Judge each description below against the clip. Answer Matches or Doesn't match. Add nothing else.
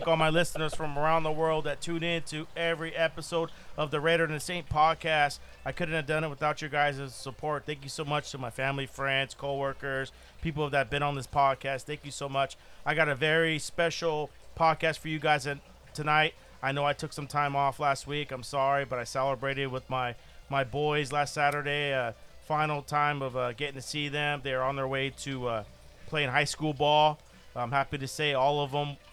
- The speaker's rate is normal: Doesn't match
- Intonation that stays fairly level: Matches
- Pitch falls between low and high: Matches